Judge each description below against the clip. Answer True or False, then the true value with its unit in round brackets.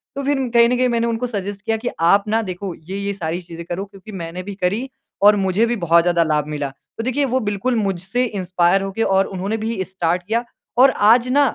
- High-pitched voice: True (200 Hz)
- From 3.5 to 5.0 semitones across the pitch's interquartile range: True (4.5 semitones)